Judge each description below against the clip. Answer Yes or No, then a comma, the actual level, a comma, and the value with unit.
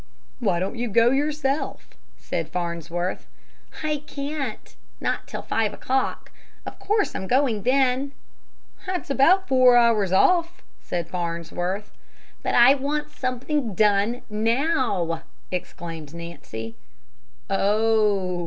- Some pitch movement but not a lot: No, wide, 7.1 semitones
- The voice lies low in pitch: No, high, 230 Hz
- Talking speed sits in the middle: No, slow, 110 wpm